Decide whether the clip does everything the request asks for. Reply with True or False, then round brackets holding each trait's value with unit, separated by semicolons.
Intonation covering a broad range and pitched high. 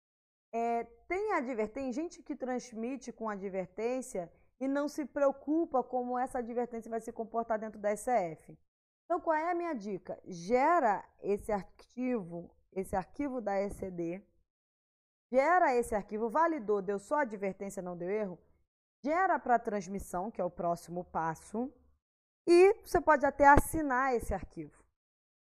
True (6.0 semitones; 235 Hz)